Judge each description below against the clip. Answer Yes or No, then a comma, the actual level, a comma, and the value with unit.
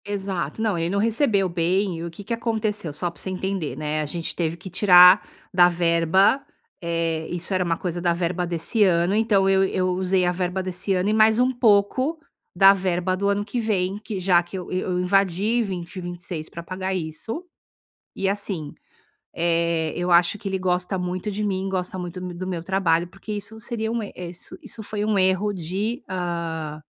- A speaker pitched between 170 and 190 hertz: Yes, medium, 185 Hz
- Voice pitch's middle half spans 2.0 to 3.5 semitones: Yes, average, 2.8 semitones